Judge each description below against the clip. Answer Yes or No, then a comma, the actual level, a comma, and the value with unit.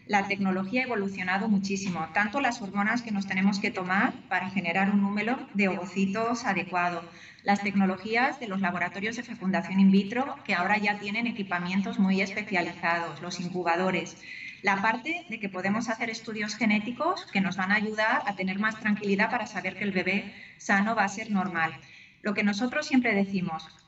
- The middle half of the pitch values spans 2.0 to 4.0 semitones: Yes, average, 2.8 semitones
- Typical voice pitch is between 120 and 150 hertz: No, high, 200 Hz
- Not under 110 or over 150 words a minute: No, average, 175 wpm